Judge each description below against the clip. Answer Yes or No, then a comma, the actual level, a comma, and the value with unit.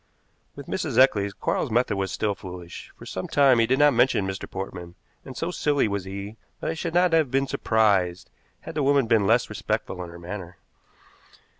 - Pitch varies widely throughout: Yes, wide, 6.0 semitones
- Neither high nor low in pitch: No, low, 110 Hz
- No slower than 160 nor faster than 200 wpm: Yes, average, 195 wpm